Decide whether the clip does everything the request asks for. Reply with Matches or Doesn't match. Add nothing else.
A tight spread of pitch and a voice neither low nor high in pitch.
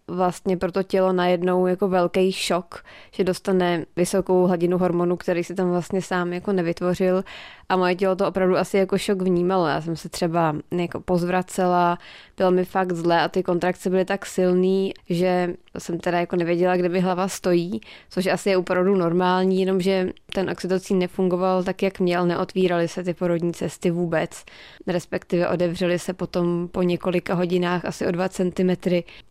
Matches